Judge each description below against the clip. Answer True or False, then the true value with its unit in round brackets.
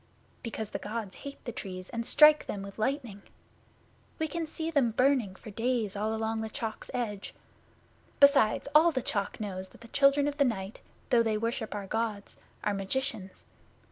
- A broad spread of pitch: False (4.8 semitones)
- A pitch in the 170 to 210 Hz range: False (225 Hz)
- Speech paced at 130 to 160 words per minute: False (175 wpm)